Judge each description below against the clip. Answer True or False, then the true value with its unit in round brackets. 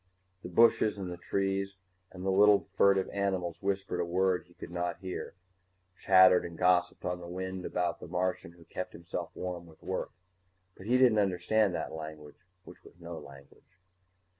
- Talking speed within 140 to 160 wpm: False (175 wpm)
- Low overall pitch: True (90 Hz)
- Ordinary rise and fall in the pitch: False (2.0 semitones)